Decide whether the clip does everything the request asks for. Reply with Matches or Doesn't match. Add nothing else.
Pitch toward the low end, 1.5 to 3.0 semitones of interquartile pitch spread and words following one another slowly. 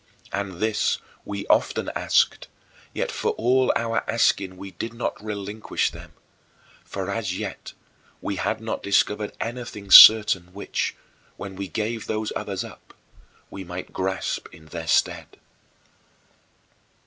Matches